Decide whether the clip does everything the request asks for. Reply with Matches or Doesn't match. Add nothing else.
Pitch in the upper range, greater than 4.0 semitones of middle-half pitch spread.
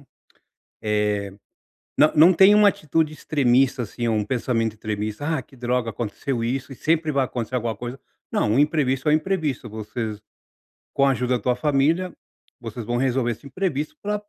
Doesn't match